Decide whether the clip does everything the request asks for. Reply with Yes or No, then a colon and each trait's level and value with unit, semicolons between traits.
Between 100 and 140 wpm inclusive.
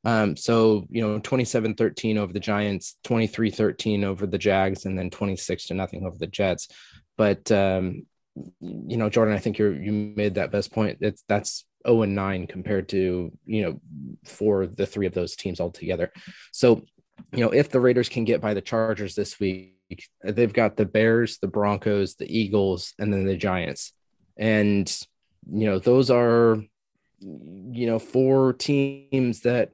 No: average, 175 wpm